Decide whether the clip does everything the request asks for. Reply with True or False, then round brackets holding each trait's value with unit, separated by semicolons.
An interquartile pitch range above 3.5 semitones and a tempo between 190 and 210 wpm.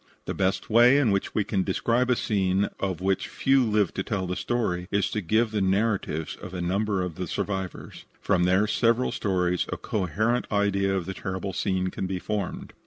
False (2.7 semitones; 200 wpm)